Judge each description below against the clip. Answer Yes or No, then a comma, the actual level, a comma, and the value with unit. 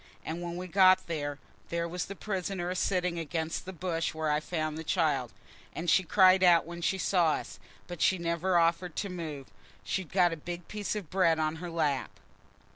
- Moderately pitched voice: Yes, medium, 170 Hz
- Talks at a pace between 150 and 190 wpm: No, average, 200 wpm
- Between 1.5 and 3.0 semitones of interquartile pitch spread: Yes, narrow, 2.4 semitones